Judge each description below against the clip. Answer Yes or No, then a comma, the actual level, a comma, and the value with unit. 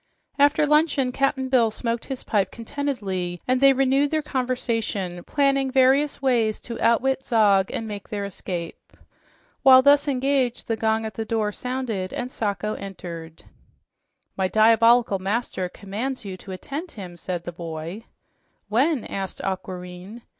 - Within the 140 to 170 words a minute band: Yes, average, 145 wpm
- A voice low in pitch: No, high, 225 Hz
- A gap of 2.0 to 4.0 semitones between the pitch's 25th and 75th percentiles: No, wide, 5.4 semitones